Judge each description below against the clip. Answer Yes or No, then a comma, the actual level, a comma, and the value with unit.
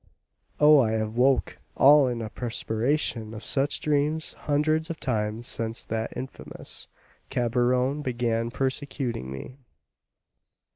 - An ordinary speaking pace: No, slow, 115 wpm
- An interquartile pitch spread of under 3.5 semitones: No, average, 4.0 semitones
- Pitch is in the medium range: No, low, 125 Hz